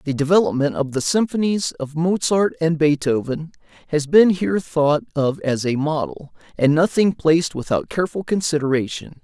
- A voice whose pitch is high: No, medium, 160 Hz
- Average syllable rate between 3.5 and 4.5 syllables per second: No, 5.0 syllables/s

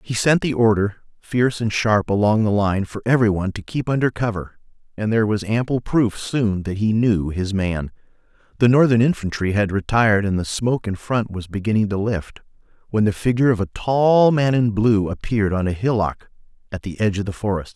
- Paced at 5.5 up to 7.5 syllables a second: Yes, 5.6 syllables/s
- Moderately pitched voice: No, low, 105 Hz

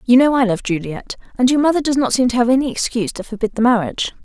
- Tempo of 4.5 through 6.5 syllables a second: No, 7.0 syllables/s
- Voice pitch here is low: No, high, 240 Hz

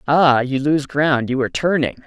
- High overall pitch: No, medium, 140 Hz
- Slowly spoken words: No, fast, 205 wpm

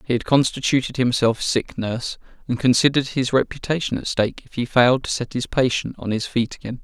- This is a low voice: Yes, low, 125 Hz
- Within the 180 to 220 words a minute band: Yes, average, 200 wpm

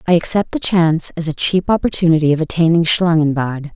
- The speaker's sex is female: Yes, female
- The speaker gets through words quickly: No, average, 175 wpm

